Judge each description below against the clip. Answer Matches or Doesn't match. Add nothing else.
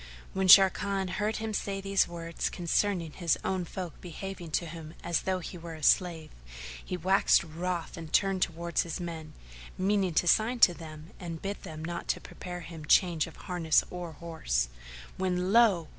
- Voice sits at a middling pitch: Matches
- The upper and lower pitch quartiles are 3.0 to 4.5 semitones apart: Doesn't match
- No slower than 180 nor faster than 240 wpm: Doesn't match